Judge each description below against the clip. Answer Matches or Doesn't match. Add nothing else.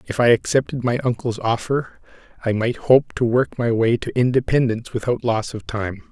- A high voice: Doesn't match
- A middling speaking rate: Matches